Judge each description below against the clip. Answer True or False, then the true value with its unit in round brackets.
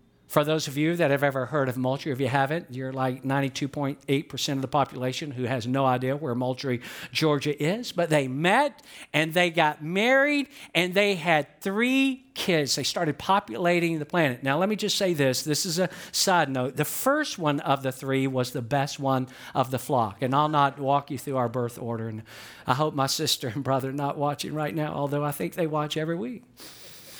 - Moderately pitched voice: True (145 Hz)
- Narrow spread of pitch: False (4.0 semitones)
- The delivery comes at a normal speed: False (210 wpm)